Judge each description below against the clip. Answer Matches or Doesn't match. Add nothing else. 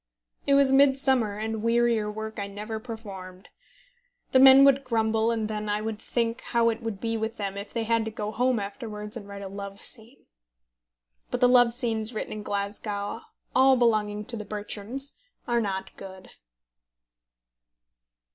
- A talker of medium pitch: Doesn't match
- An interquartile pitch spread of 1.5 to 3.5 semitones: Matches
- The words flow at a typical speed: Matches